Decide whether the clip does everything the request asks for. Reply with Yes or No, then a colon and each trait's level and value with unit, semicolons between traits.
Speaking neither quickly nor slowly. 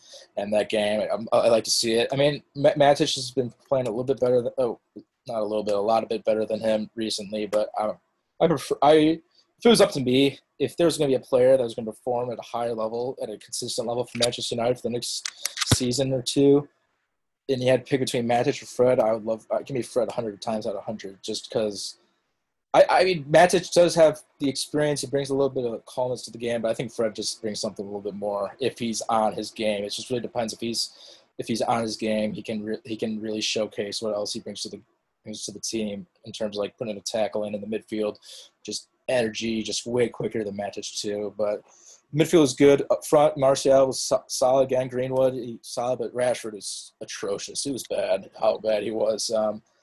No: fast, 245 wpm